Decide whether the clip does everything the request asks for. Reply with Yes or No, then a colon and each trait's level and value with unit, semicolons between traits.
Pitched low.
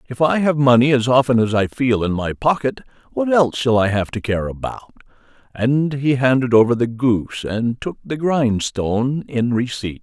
Yes: low, 125 Hz